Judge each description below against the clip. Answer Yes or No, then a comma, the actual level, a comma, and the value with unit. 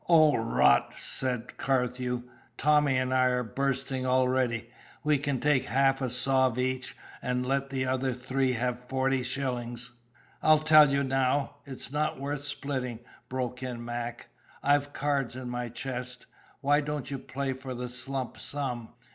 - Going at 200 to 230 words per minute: No, average, 155 wpm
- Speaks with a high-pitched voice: No, low, 130 Hz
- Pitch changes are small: Yes, narrow, 1.7 semitones